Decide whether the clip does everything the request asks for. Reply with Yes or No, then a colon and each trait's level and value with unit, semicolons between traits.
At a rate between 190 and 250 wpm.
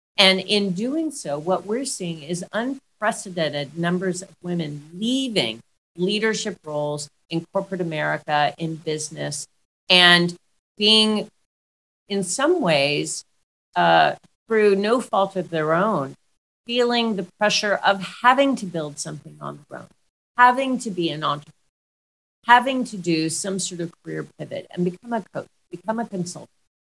No: average, 140 wpm